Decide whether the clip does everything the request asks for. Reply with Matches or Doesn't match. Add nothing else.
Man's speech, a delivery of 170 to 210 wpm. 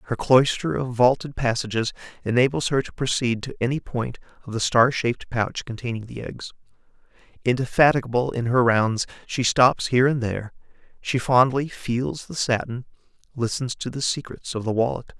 Doesn't match